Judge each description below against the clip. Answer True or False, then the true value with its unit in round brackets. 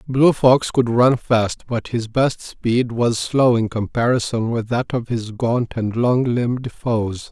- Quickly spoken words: False (180 wpm)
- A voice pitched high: False (120 Hz)